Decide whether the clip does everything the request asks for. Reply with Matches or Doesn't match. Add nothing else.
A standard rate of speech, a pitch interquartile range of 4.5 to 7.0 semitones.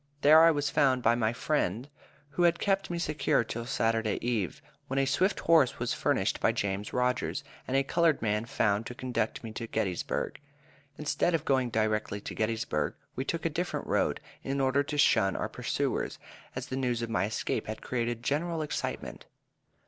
Matches